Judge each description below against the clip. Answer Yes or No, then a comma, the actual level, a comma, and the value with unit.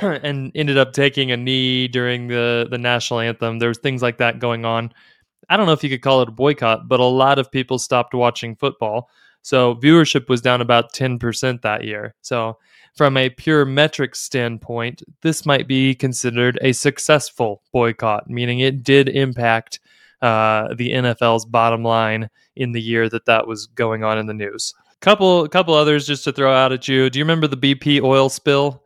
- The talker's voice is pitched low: Yes, low, 125 Hz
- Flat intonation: No, average, 3.0 semitones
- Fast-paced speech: No, average, 195 wpm